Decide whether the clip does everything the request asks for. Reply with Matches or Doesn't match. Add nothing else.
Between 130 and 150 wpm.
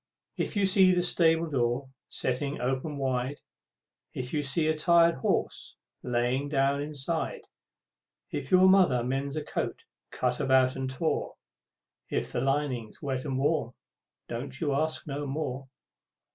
Matches